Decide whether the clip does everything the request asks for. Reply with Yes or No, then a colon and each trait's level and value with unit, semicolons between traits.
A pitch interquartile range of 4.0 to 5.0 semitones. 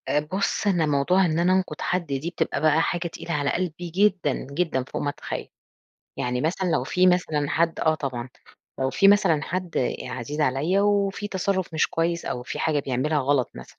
Yes: average, 4.3 semitones